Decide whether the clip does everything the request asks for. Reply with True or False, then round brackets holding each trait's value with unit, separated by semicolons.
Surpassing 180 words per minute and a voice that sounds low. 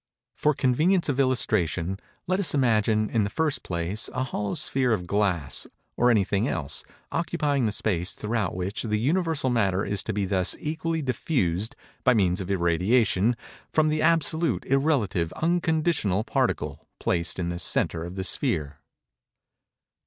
False (155 wpm; 110 Hz)